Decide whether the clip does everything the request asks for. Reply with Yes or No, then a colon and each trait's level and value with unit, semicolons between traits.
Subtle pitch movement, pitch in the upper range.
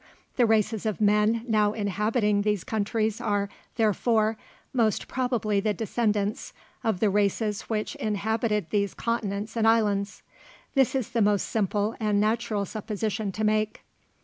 Yes: narrow, 1.4 semitones; high, 215 Hz